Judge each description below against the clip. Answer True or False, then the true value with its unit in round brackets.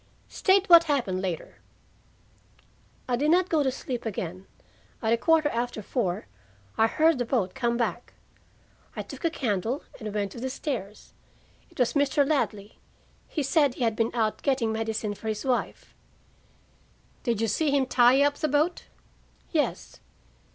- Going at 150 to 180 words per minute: True (160 wpm)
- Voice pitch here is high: True (245 Hz)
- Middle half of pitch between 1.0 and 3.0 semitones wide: False (4.6 semitones)